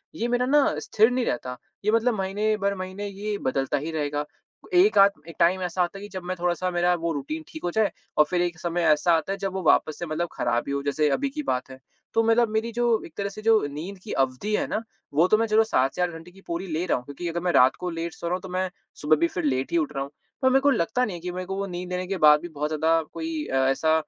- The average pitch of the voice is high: No, medium, 175 Hz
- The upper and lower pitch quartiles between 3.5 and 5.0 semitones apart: Yes, average, 4.4 semitones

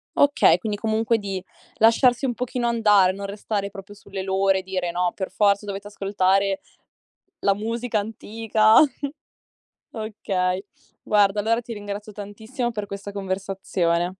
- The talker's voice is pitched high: Yes, high, 205 Hz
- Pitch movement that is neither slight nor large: No, narrow, 2.3 semitones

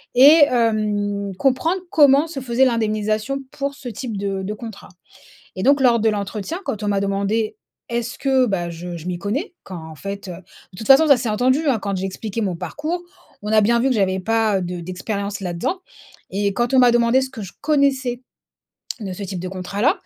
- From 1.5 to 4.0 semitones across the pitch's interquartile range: No, average, 4.7 semitones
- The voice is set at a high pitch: Yes, high, 220 Hz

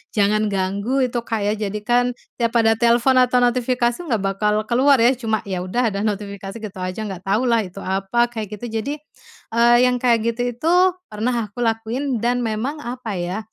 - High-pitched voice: Yes, high, 230 Hz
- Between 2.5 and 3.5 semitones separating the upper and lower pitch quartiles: Yes, average, 2.8 semitones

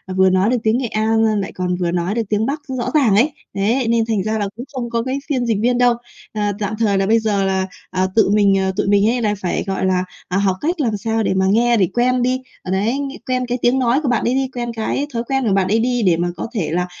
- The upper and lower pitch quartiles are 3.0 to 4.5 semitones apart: Yes, average, 3.9 semitones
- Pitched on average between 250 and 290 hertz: No, high, 220 Hz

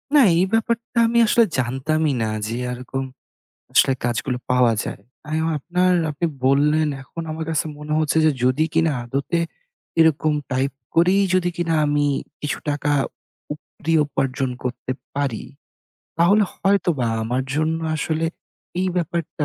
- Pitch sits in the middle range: Yes, medium, 150 Hz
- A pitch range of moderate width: Yes, average, 4.1 semitones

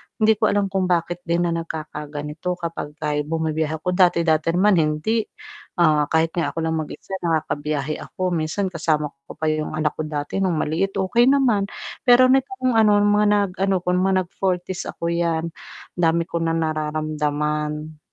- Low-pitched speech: No, medium, 170 Hz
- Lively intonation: No, average, 3.8 semitones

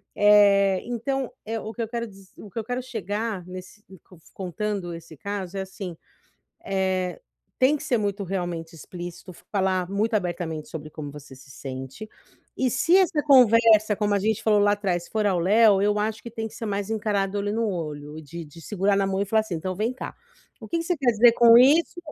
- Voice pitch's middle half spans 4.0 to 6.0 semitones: No, average, 3.6 semitones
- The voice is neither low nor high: No, high, 205 Hz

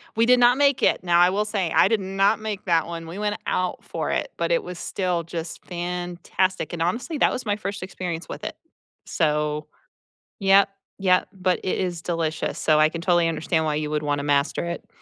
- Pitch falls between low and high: Yes, medium, 180 Hz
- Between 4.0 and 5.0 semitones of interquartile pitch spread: No, average, 3.3 semitones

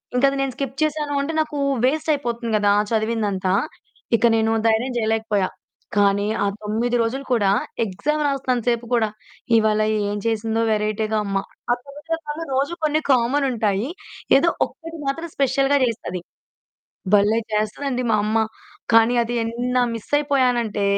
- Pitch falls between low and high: No, high, 235 Hz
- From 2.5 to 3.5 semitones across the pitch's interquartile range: No, average, 4.3 semitones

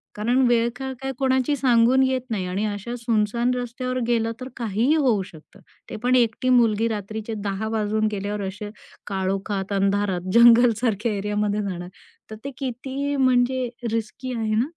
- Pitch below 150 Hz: No, high, 230 Hz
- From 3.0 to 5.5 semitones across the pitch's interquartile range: Yes, average, 3.4 semitones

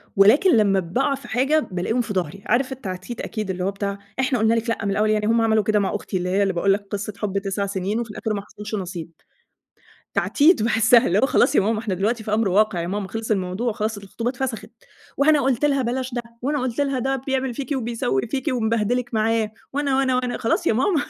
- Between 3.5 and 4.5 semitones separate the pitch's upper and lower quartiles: Yes, average, 4.0 semitones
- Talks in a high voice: Yes, high, 220 Hz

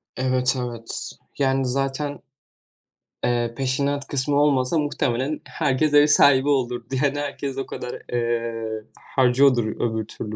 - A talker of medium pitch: No, low, 130 Hz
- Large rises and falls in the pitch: No, average, 2.9 semitones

